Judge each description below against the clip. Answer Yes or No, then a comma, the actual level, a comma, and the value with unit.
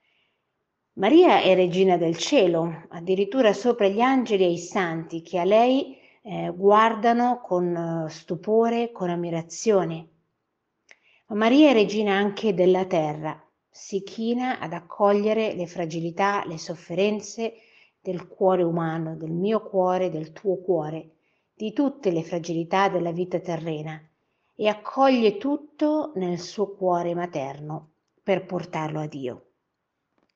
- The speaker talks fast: No, average, 125 wpm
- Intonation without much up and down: No, average, 4.1 semitones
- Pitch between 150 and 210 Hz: Yes, medium, 185 Hz